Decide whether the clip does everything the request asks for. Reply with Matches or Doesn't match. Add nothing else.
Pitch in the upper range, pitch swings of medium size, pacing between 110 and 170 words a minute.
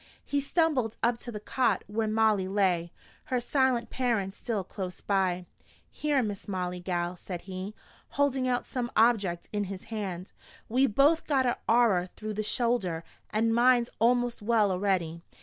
Matches